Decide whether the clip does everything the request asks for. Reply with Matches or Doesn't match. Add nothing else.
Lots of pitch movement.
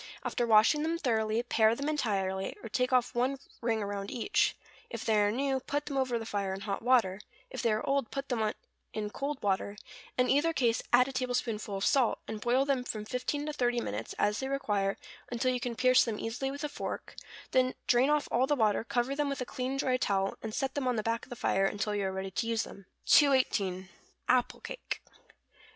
Doesn't match